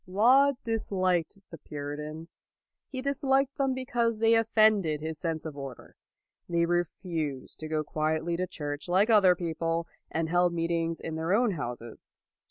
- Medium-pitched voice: Yes, medium, 170 Hz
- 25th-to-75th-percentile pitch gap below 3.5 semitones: No, wide, 5.6 semitones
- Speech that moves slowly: No, average, 160 wpm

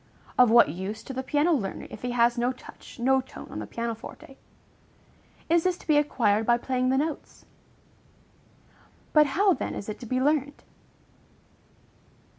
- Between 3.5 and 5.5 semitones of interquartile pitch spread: Yes, average, 3.9 semitones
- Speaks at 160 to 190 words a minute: Yes, average, 170 wpm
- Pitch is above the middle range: Yes, very high, 255 Hz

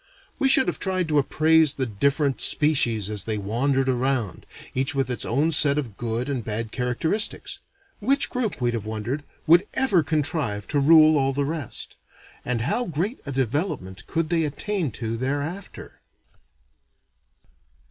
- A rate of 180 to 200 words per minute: No, average, 155 wpm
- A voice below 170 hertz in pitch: Yes, medium, 140 Hz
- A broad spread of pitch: No, average, 5.0 semitones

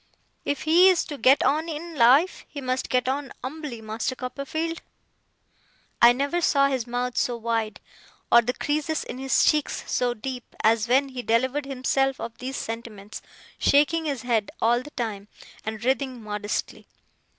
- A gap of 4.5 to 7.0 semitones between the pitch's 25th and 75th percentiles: No, average, 3.6 semitones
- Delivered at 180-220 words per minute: No, average, 160 wpm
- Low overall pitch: No, very high, 255 Hz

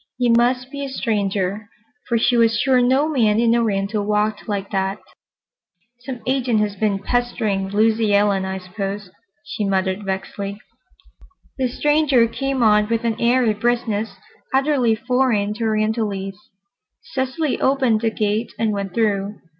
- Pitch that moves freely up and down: No, average, 3.3 semitones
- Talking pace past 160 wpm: No, average, 145 wpm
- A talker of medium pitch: No, high, 220 Hz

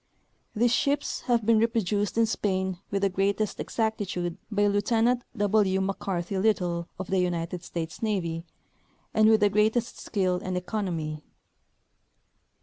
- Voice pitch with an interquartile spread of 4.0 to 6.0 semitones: No, average, 3.3 semitones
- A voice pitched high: Yes, high, 200 Hz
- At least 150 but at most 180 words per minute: No, slow, 135 wpm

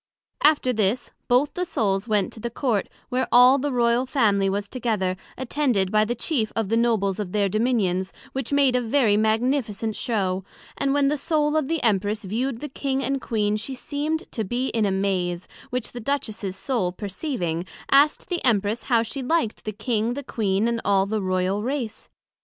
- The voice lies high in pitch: Yes, high, 230 Hz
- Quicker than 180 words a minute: Yes, average, 190 wpm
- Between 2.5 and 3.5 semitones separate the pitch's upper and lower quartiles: No, average, 4.6 semitones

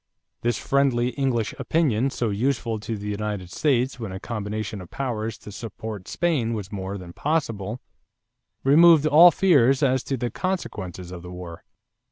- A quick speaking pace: No, average, 160 wpm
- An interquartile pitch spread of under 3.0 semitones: No, average, 5.0 semitones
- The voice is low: Yes, low, 115 Hz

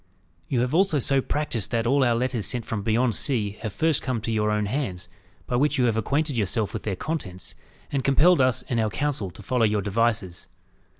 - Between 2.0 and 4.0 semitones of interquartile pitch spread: No, average, 4.4 semitones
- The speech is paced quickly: Yes, fast, 215 wpm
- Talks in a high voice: No, low, 120 Hz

